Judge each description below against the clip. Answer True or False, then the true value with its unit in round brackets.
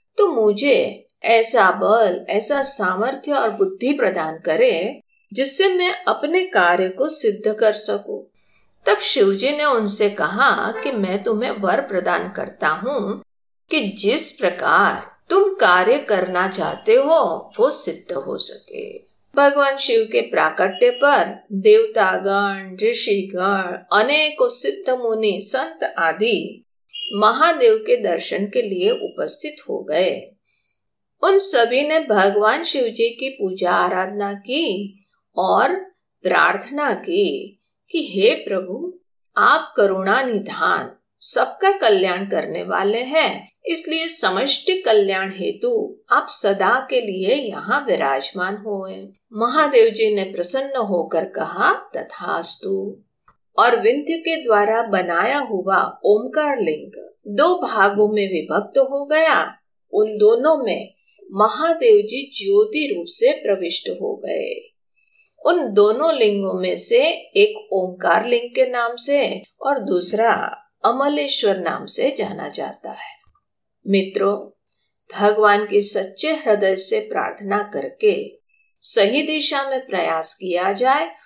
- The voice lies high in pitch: True (260 Hz)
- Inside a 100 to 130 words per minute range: True (120 wpm)